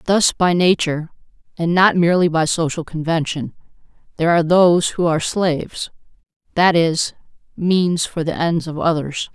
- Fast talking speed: No, average, 140 wpm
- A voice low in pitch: No, medium, 170 Hz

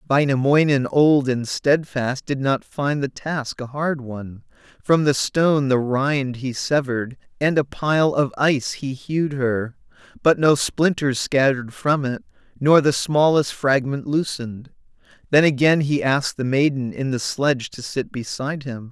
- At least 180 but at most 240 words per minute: No, average, 160 wpm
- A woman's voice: No, male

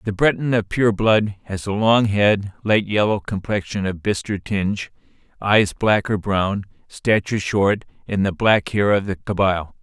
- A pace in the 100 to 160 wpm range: No, average, 170 wpm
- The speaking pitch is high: No, low, 100 Hz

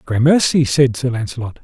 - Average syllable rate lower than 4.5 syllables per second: No, 5.3 syllables/s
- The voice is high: No, low, 125 Hz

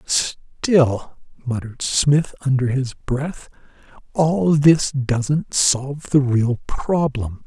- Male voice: Yes, male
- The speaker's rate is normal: No, slow, 105 wpm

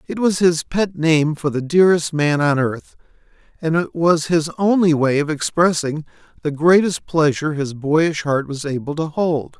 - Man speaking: Yes, male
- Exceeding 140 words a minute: Yes, average, 180 wpm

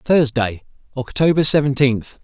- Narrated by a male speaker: Yes, male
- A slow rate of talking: Yes, slow, 80 wpm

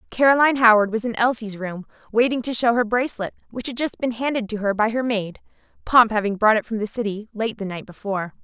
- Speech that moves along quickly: Yes, fast, 230 wpm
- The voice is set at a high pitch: Yes, high, 225 Hz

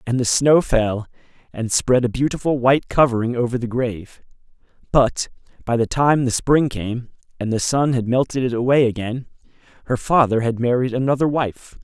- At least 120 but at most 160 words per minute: No, average, 170 wpm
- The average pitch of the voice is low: Yes, low, 125 Hz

